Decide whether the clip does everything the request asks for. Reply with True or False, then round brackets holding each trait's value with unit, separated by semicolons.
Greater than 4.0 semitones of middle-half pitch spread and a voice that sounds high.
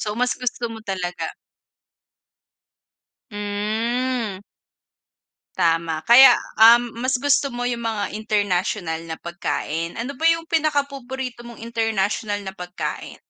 True (4.4 semitones; 225 Hz)